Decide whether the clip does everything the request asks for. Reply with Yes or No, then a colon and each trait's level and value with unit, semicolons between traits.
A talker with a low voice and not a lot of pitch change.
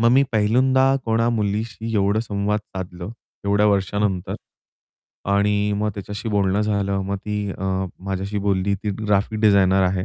Yes: low, 100 Hz; narrow, 1.6 semitones